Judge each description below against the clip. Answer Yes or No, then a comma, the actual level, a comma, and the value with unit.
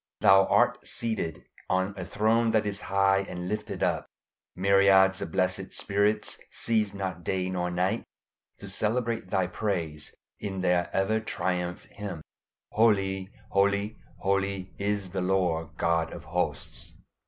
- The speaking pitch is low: Yes, very low, 95 Hz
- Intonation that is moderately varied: No, narrow, 2.0 semitones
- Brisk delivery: No, slow, 135 wpm